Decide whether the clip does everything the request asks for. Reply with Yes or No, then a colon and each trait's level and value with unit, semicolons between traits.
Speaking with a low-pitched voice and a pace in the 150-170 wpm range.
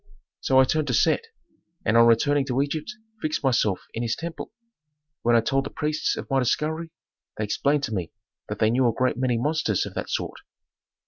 No: low, 130 Hz; average, 200 wpm